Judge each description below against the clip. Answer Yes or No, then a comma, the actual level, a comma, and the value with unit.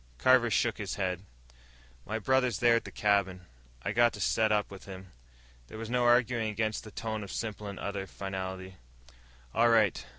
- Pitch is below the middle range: Yes, low, 105 Hz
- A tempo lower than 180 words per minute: No, average, 185 wpm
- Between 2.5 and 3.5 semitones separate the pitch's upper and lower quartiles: Yes, average, 3.2 semitones